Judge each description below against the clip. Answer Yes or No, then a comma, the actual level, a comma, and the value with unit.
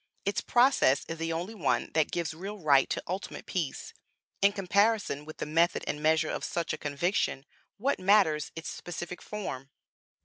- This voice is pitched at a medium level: Yes, medium, 170 Hz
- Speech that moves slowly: No, average, 170 wpm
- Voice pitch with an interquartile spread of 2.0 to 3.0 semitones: No, average, 4.5 semitones